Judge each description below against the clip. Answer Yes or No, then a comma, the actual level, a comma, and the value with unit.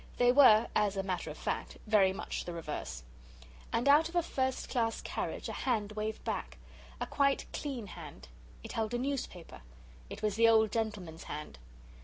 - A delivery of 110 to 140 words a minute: No, average, 180 wpm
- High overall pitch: Yes, high, 220 Hz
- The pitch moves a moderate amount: Yes, average, 4.7 semitones